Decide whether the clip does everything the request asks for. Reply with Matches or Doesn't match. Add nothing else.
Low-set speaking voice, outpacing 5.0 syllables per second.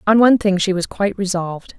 Doesn't match